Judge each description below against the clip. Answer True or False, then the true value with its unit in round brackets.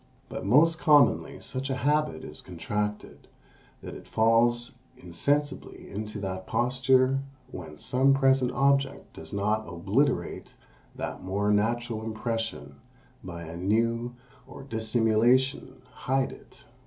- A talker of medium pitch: False (115 Hz)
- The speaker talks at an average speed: False (115 wpm)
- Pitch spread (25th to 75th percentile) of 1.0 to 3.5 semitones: False (4.4 semitones)